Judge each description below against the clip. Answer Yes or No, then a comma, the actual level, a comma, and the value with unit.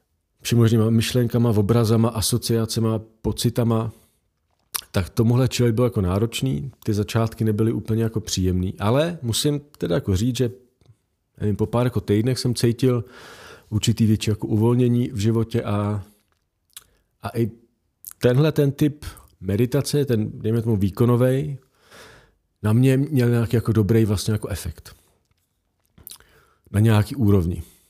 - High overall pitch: No, low, 115 Hz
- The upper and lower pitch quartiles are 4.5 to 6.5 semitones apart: No, average, 2.8 semitones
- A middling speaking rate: Yes, average, 125 wpm